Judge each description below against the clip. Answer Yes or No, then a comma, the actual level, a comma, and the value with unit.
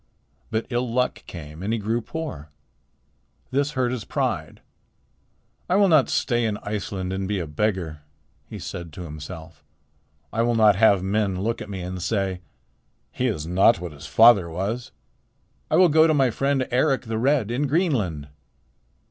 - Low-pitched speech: Yes, low, 110 Hz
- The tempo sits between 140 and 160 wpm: No, average, 170 wpm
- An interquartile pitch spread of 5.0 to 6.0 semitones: Yes, wide, 5.6 semitones